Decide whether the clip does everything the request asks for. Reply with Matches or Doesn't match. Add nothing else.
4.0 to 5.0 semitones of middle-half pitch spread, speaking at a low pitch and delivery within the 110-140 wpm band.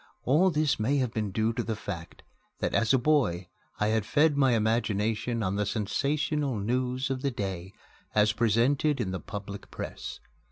Doesn't match